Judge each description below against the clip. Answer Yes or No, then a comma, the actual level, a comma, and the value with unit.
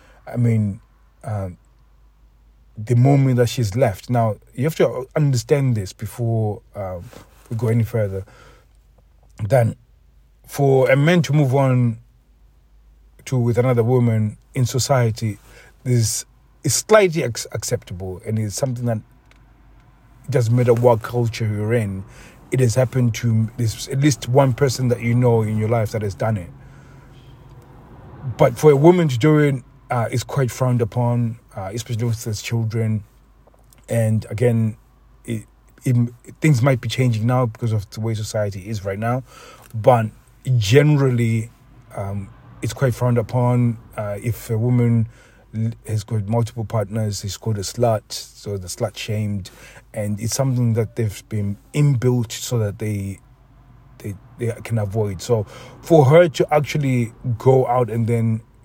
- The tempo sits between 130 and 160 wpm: Yes, average, 150 wpm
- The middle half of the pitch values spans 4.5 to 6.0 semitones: No, narrow, 2.6 semitones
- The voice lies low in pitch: Yes, low, 120 Hz